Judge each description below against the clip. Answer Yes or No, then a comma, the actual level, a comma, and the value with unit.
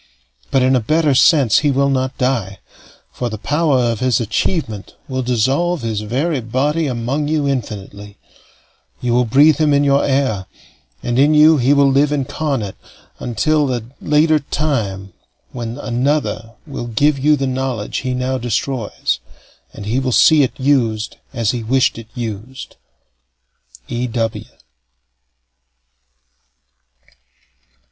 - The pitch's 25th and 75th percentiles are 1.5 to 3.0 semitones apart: No, average, 3.8 semitones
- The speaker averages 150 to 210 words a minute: No, average, 140 wpm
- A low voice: Yes, low, 130 Hz